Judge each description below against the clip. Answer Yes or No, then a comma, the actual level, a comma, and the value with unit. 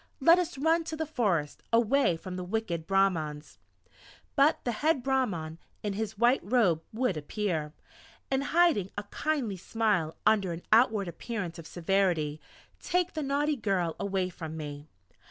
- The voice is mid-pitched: No, high, 205 Hz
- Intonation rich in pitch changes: Yes, wide, 7.7 semitones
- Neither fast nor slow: Yes, average, 155 wpm